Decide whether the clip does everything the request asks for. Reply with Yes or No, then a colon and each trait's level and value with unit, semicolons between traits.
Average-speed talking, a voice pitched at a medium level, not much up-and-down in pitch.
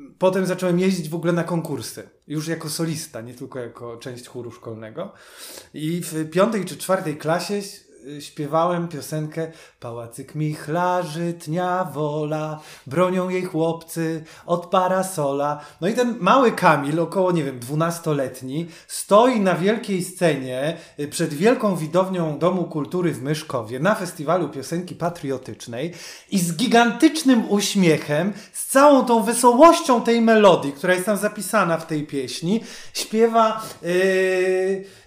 No: average, 130 wpm; medium, 170 Hz; average, 4.0 semitones